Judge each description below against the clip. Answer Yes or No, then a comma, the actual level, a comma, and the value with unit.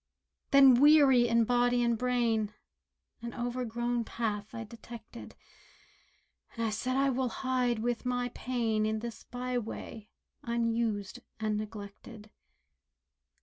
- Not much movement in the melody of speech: Yes, narrow, 2.0 semitones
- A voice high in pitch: Yes, high, 235 Hz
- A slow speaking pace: Yes, slow, 115 wpm